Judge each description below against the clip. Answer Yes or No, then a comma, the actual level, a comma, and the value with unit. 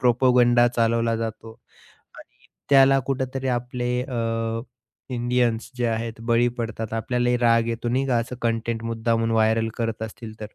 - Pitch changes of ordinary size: No, narrow, 1.3 semitones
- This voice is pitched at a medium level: No, low, 115 Hz